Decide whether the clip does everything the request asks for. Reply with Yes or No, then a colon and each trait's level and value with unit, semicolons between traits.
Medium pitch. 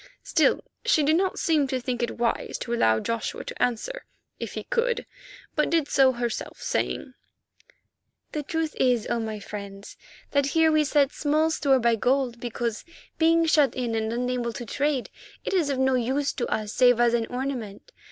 No: very high, 260 Hz